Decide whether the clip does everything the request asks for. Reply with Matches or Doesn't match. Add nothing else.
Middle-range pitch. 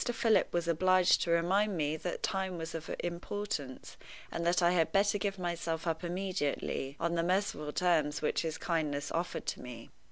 Matches